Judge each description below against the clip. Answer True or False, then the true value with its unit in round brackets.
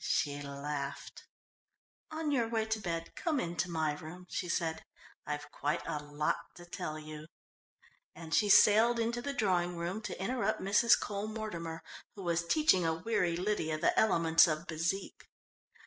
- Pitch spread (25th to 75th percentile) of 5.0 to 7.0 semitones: True (5.3 semitones)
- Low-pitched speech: False (175 Hz)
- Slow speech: False (165 wpm)